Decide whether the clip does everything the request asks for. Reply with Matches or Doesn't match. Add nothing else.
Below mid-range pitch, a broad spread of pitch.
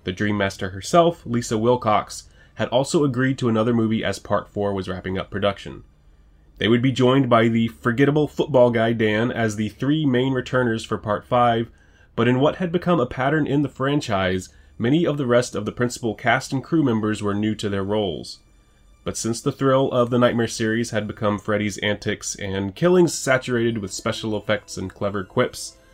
Doesn't match